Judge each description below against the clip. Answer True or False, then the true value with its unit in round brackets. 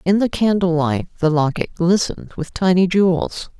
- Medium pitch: True (175 Hz)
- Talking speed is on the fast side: False (165 wpm)